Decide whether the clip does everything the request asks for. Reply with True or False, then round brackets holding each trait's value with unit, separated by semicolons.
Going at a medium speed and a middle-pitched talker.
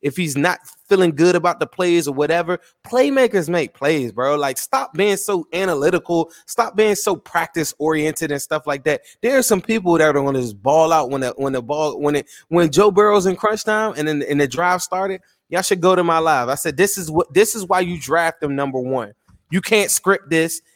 False (230 wpm; 170 Hz)